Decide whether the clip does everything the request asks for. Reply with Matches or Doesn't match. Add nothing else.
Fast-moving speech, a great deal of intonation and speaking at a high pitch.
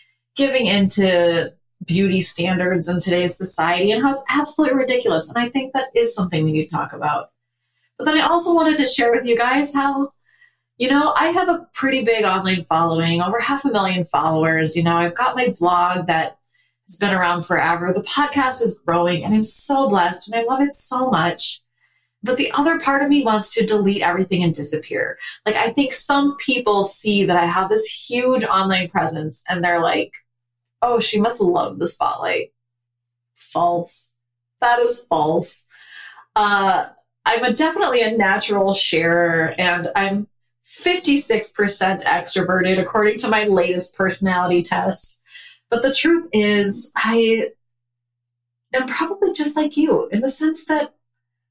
Doesn't match